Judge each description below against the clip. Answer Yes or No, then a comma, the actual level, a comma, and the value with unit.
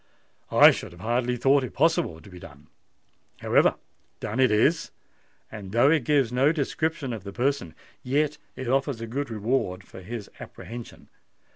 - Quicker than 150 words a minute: Yes, average, 160 wpm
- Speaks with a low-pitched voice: Yes, low, 125 Hz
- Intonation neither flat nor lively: Yes, average, 4.8 semitones